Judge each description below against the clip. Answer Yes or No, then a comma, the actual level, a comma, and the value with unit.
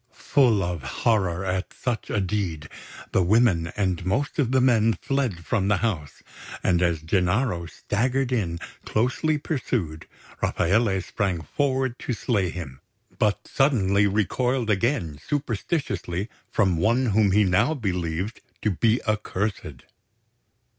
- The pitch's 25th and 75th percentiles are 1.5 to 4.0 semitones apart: No, wide, 5.4 semitones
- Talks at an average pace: No, slow, 130 wpm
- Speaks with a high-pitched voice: No, low, 105 Hz